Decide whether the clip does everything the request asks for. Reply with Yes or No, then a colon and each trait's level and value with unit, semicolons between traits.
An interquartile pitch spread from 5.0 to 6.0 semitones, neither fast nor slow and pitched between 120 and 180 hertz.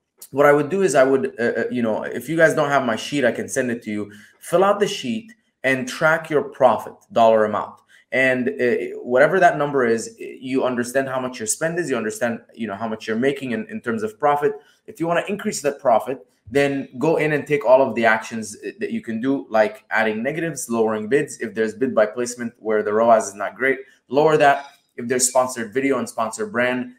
No: average, 5.3 semitones; fast, 230 wpm; low, 135 Hz